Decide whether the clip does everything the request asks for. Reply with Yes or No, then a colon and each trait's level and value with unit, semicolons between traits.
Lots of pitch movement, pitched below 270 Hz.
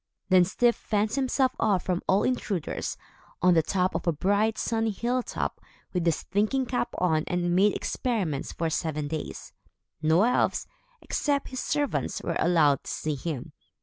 Yes: wide, 6.0 semitones; high, 190 Hz